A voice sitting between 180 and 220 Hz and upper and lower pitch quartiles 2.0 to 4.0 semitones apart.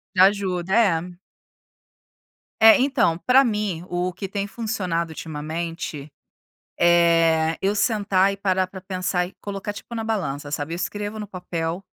Yes: medium, 185 Hz; average, 3.5 semitones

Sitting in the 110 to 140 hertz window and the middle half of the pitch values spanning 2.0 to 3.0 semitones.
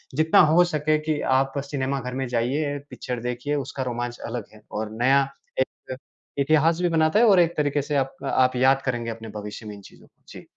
No: low, 135 Hz; average, 3.8 semitones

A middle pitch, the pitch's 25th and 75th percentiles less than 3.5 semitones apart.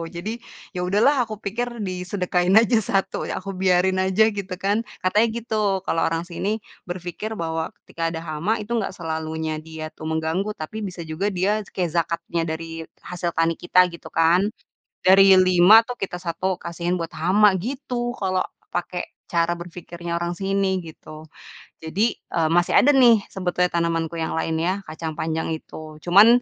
Yes: medium, 180 Hz; average, 2.8 semitones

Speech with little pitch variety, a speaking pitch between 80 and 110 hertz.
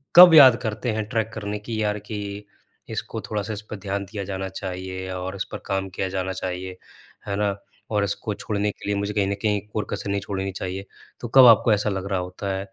Yes: narrow, 1.7 semitones; low, 100 Hz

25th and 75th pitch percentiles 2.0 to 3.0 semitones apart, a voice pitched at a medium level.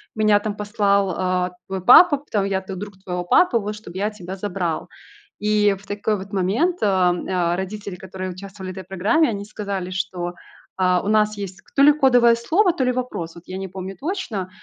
No: narrow, 2.4 semitones; high, 200 Hz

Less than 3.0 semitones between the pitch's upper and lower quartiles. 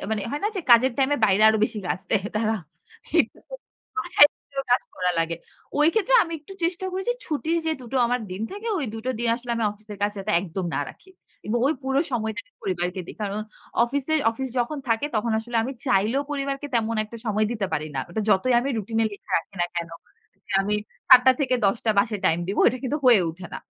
No: average, 5.1 semitones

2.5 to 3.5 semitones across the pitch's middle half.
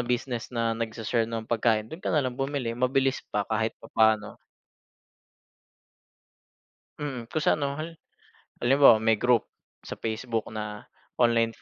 Yes: average, 3.0 semitones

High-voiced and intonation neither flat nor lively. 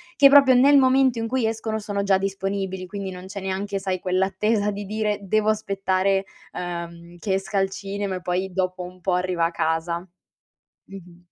No: high, 195 Hz; narrow, 2.3 semitones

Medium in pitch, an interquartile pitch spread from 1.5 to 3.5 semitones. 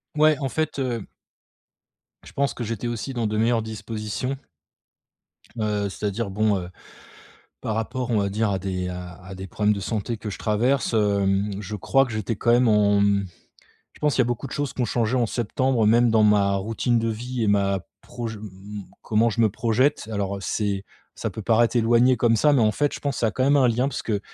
No: low, 110 Hz; average, 3.0 semitones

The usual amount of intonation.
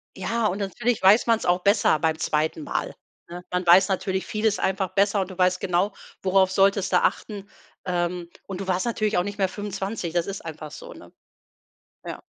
No: narrow, 2.2 semitones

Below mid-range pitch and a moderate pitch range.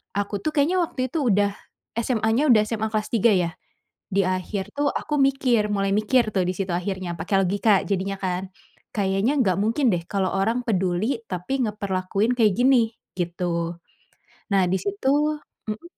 No: high, 205 Hz; average, 4.6 semitones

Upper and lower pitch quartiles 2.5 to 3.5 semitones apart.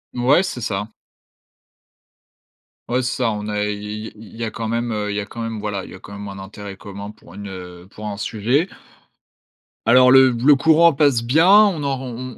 No: average, 4.0 semitones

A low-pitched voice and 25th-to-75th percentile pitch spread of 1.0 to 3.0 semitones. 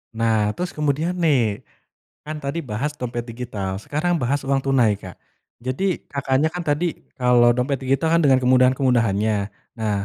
No: low, 130 Hz; average, 4.4 semitones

